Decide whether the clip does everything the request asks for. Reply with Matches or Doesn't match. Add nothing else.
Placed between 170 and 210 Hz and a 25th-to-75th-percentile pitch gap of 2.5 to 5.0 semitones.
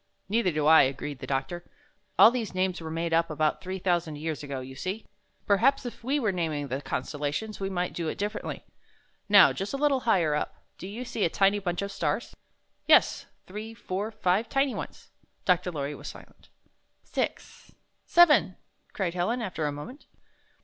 Doesn't match